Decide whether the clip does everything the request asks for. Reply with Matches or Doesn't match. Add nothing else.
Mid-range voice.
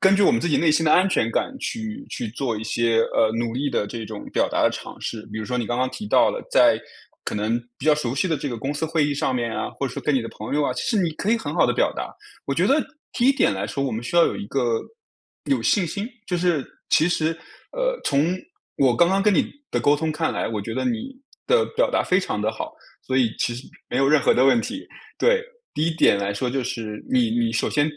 Matches